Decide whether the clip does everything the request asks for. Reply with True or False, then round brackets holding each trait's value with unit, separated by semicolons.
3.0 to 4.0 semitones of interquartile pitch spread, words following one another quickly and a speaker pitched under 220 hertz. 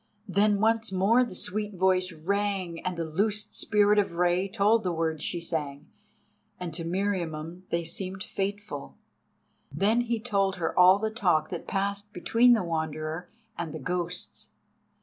False (3.4 semitones; 155 wpm; 185 Hz)